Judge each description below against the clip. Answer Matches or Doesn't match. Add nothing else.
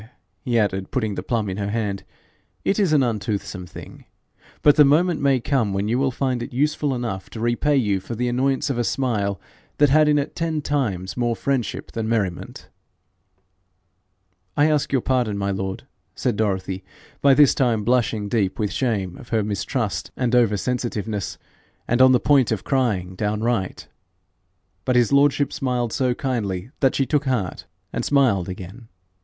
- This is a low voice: Matches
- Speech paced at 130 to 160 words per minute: Doesn't match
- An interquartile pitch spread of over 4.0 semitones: Matches